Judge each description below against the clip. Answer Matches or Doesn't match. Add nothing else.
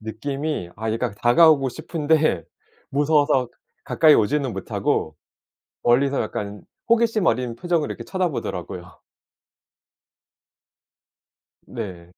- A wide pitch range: Matches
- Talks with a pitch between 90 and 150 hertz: Matches